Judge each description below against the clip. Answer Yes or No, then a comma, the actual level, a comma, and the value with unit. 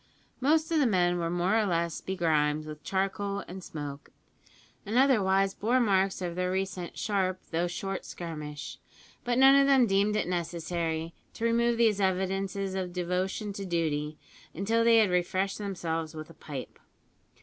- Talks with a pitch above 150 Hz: Yes, high, 190 Hz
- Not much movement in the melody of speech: No, average, 3.4 semitones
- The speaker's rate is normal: Yes, average, 160 wpm